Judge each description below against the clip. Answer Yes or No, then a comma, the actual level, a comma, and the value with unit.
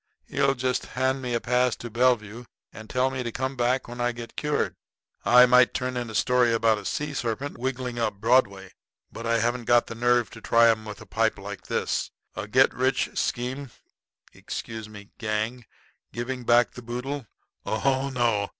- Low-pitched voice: Yes, low, 120 Hz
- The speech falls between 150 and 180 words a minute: No, average, 190 wpm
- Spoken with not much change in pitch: Yes, narrow, 2.0 semitones